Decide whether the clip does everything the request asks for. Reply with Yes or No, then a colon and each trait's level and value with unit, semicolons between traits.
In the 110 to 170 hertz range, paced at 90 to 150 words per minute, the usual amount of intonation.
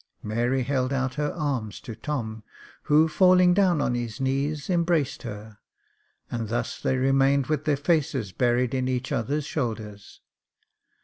Yes: low, 135 Hz; average, 145 wpm; average, 3.9 semitones